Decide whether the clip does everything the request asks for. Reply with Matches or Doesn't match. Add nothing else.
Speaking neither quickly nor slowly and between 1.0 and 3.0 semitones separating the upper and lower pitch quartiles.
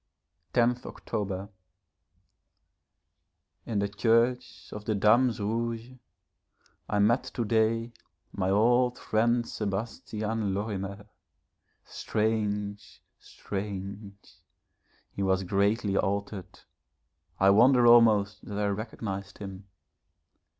Doesn't match